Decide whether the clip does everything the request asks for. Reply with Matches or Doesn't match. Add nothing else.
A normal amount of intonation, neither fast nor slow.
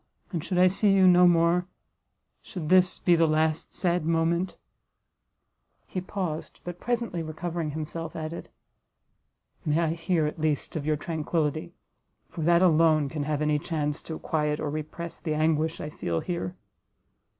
Doesn't match